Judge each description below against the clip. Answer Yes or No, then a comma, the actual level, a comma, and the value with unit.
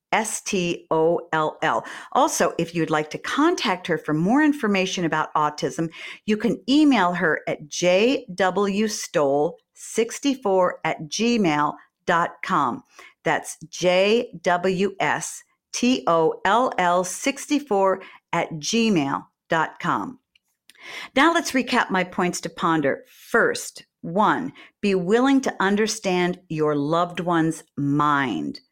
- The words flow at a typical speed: No, slow, 90 wpm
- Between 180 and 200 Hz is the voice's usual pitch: Yes, medium, 185 Hz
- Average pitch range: No, wide, 6.0 semitones